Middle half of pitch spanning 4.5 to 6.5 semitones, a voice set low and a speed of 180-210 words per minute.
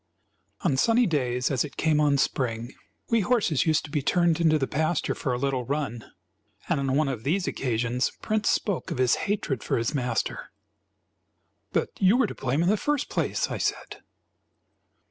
No: wide, 5.6 semitones; medium, 145 Hz; average, 185 wpm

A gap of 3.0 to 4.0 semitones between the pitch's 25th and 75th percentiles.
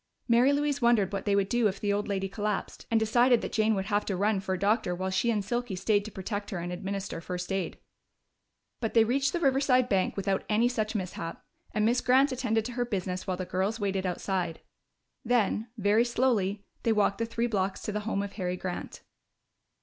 Yes: average, 3.6 semitones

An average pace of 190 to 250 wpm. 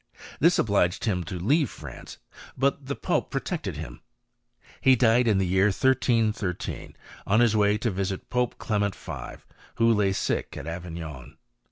No: average, 155 wpm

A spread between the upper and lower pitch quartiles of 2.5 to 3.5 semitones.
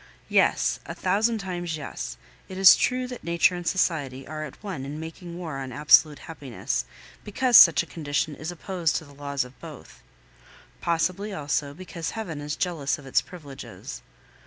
No: average, 4.2 semitones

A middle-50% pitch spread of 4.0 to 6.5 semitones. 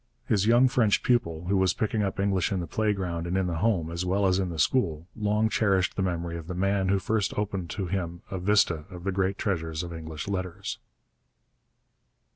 No: average, 2.9 semitones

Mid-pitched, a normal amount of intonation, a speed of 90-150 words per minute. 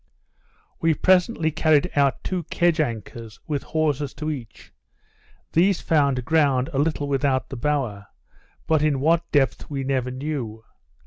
Yes: medium, 145 Hz; average, 3.3 semitones; average, 140 wpm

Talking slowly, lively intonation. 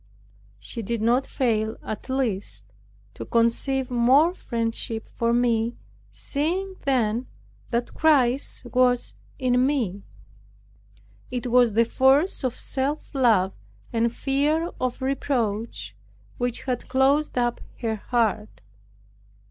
No: slow, 110 wpm; average, 2.8 semitones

